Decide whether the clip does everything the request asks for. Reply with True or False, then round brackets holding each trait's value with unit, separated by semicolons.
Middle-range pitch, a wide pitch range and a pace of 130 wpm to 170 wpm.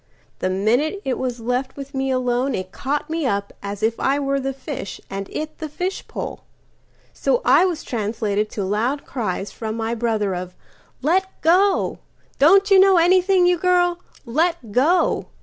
False (265 Hz; 7.5 semitones; 150 wpm)